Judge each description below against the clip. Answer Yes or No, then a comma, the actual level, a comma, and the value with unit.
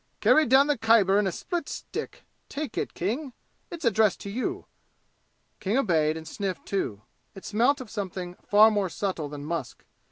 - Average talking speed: Yes, average, 170 wpm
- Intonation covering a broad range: Yes, wide, 6.0 semitones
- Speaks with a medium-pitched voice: No, high, 205 Hz